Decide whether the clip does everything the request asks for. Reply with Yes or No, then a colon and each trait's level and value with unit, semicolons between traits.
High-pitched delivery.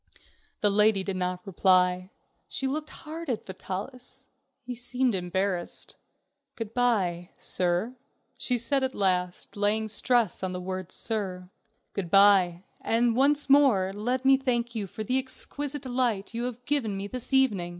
Yes: high, 215 Hz